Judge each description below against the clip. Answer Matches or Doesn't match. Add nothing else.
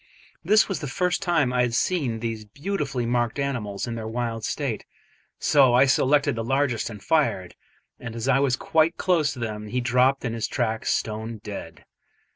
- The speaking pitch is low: Matches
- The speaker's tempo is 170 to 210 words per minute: Matches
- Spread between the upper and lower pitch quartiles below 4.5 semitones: Matches